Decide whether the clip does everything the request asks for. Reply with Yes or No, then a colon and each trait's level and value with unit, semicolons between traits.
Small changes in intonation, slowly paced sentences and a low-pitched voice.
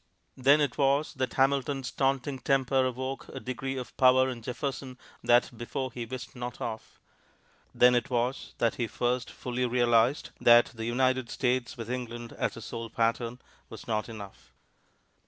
No: narrow, 1.9 semitones; average, 160 wpm; low, 125 Hz